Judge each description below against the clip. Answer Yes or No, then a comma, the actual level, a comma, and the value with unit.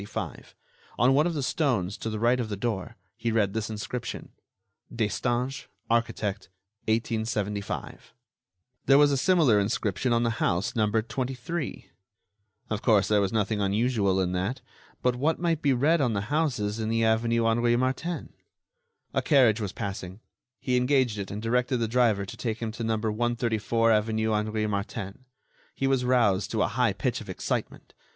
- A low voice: Yes, low, 115 Hz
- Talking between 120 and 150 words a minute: No, average, 165 wpm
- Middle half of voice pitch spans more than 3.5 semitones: No, average, 3.1 semitones